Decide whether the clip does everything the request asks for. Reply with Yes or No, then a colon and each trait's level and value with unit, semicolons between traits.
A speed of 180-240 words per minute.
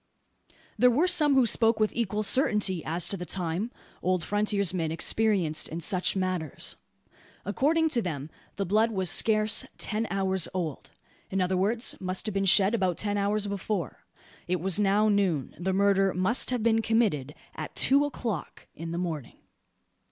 No: average, 165 wpm